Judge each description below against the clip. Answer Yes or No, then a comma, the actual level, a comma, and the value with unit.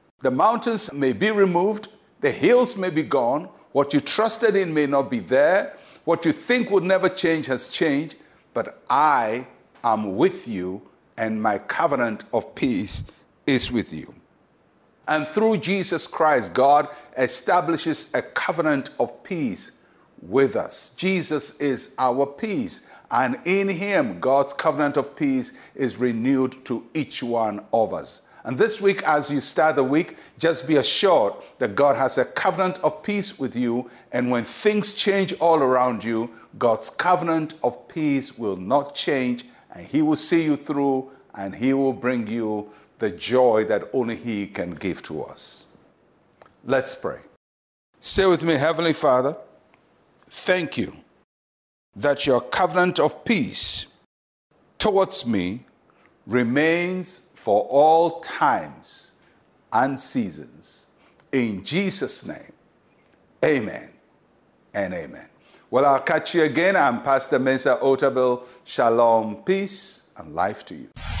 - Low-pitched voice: No, medium, 145 Hz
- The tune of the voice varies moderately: No, wide, 6.7 semitones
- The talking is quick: No, average, 140 wpm